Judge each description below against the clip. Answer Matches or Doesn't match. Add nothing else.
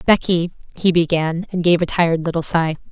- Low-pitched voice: Doesn't match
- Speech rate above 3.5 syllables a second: Matches